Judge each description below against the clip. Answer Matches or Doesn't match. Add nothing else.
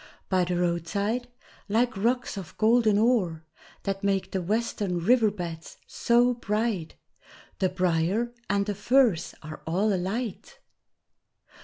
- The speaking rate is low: Matches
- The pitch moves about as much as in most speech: Matches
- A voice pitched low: Doesn't match